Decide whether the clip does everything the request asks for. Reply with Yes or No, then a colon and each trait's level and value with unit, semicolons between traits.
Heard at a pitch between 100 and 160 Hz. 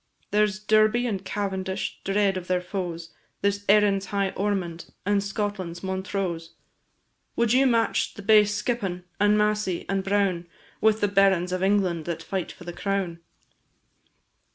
No: high, 195 Hz